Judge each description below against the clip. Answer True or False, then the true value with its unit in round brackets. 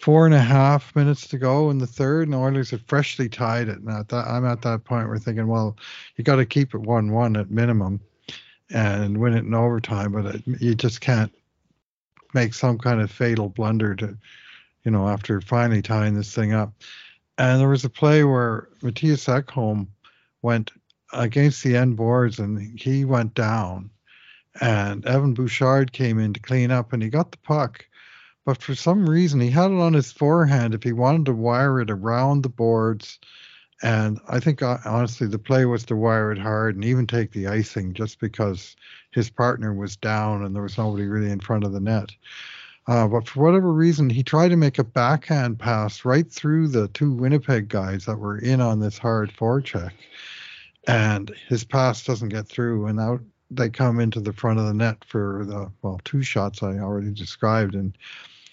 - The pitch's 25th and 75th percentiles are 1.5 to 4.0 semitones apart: True (3.4 semitones)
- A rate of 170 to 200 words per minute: True (195 wpm)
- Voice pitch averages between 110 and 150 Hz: True (115 Hz)